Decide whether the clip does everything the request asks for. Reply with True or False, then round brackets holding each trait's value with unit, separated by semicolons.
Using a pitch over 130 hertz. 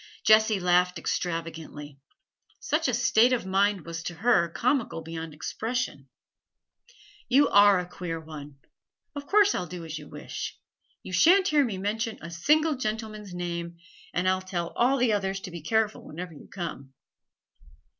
True (185 Hz)